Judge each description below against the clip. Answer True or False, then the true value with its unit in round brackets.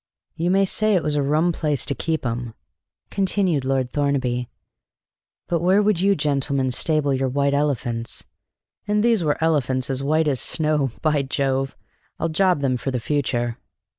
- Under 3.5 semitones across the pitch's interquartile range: False (3.9 semitones)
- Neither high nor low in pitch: True (145 Hz)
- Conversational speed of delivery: True (165 wpm)